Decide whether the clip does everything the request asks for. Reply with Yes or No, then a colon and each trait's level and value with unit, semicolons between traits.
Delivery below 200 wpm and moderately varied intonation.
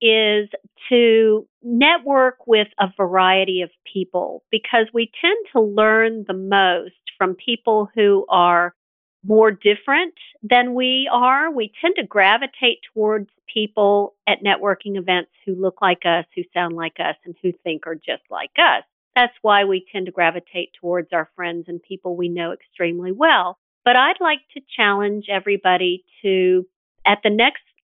Yes: average, 155 wpm; average, 4.2 semitones